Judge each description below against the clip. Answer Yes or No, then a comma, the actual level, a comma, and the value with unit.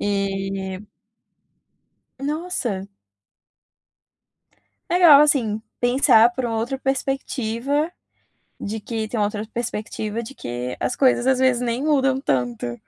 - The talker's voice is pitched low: No, high, 235 Hz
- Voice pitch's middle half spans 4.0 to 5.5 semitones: Yes, average, 4.5 semitones